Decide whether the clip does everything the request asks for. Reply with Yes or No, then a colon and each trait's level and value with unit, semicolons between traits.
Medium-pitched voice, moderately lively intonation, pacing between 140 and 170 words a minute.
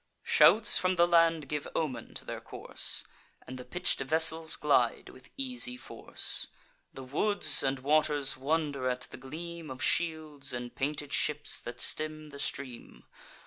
Yes: medium, 150 Hz; average, 3.6 semitones; average, 150 wpm